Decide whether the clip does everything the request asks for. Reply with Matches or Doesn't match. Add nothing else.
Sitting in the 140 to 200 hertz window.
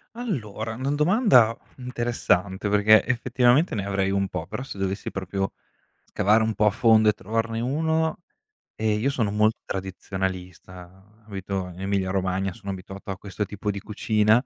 Doesn't match